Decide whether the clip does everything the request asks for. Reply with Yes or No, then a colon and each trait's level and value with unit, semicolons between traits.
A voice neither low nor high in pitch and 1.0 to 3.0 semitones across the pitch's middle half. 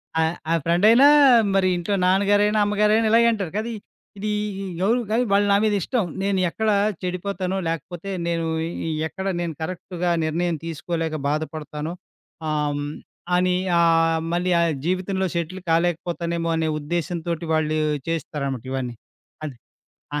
No: medium, 175 Hz; average, 3.4 semitones